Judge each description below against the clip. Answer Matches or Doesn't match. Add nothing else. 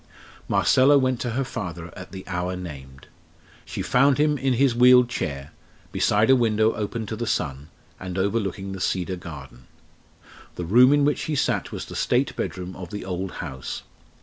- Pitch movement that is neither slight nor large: Doesn't match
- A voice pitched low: Matches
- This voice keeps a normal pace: Matches